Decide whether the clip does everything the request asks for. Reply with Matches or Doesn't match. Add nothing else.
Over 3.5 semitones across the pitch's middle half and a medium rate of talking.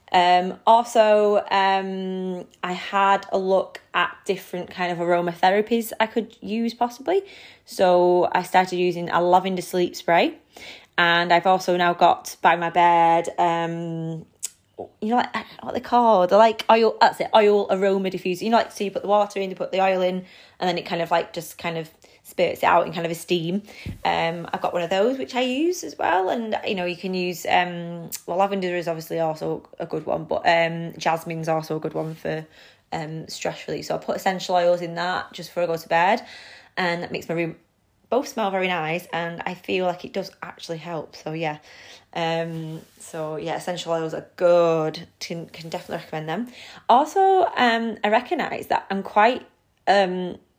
Doesn't match